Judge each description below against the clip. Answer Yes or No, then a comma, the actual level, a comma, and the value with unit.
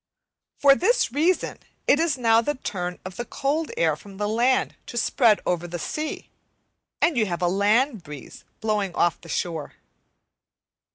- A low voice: No, high, 220 Hz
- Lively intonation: Yes, wide, 7.5 semitones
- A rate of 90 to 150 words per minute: No, average, 165 wpm